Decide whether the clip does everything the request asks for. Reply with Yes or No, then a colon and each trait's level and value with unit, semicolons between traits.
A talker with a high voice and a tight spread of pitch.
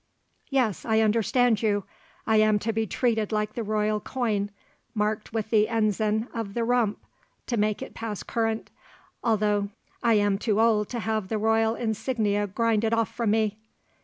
Yes: high, 220 Hz; narrow, 1.4 semitones